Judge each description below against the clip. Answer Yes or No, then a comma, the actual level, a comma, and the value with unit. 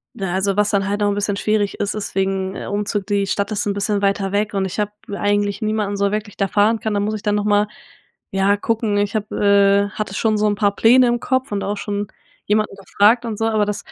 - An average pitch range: No, narrow, 1.0 semitones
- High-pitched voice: Yes, high, 205 Hz